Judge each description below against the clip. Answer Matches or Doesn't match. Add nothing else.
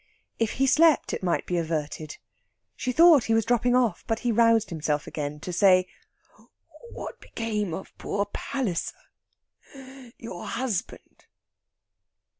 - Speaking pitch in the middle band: Doesn't match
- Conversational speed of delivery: Doesn't match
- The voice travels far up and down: Matches